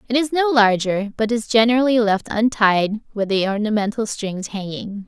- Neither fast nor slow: Yes, average, 165 wpm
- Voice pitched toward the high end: Yes, high, 220 Hz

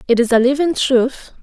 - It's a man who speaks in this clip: No, female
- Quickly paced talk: Yes, fast, 210 wpm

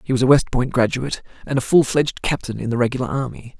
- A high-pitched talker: No, low, 125 Hz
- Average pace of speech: No, fast, 250 wpm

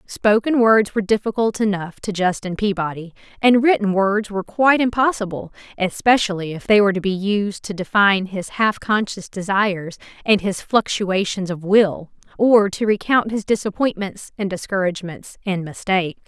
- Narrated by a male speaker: No, female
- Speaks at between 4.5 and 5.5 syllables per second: Yes, 5.1 syllables/s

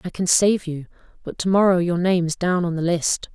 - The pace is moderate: No, fast, 250 wpm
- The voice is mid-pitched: Yes, medium, 175 Hz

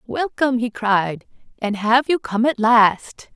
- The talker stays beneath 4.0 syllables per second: Yes, 3.7 syllables/s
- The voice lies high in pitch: Yes, high, 235 Hz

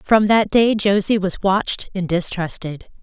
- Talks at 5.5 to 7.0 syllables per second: No, 4.4 syllables/s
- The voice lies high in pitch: Yes, high, 195 Hz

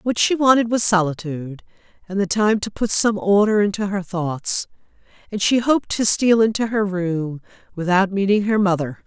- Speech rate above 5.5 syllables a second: No, 5.0 syllables/s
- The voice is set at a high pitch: Yes, high, 200 Hz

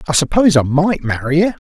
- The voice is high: No, medium, 160 Hz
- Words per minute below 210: No, fast, 215 wpm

